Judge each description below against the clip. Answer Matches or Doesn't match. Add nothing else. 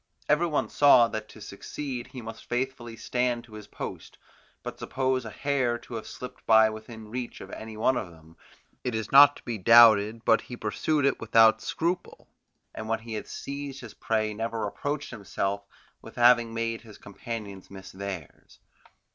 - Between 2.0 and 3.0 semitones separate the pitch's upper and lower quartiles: Matches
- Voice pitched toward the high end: Doesn't match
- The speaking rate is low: Doesn't match